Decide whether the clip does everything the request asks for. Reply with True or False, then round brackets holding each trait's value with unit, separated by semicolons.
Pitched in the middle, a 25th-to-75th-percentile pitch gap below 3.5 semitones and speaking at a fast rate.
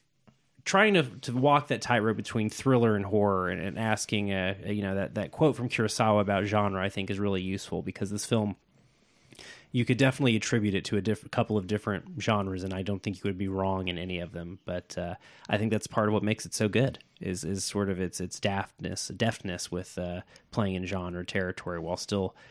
False (105 Hz; 3.1 semitones; 225 wpm)